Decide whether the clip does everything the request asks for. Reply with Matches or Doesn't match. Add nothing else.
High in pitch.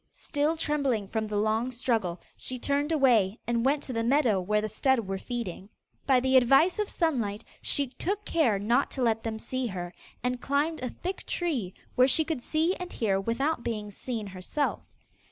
Matches